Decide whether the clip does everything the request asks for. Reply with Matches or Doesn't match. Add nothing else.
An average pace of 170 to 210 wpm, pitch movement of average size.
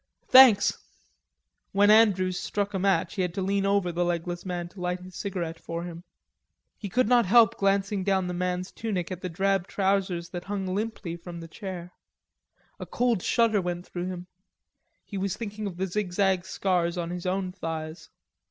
Doesn't match